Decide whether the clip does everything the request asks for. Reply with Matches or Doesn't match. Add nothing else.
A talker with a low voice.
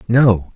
Matches